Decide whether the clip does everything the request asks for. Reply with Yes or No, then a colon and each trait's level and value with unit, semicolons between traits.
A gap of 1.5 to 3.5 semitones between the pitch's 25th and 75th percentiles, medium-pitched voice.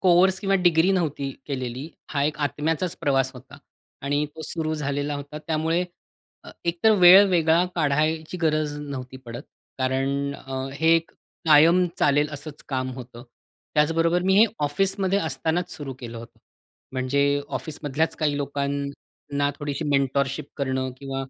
Yes: average, 2.9 semitones; medium, 145 Hz